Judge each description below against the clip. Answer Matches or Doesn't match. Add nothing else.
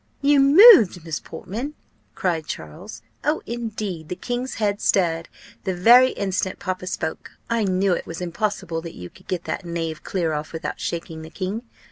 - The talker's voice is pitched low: Doesn't match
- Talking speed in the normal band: Matches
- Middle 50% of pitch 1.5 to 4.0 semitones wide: Doesn't match